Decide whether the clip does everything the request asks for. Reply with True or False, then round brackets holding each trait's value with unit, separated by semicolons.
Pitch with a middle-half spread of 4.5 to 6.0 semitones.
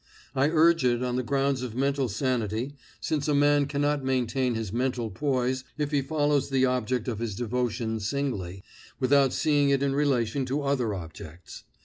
False (3.1 semitones)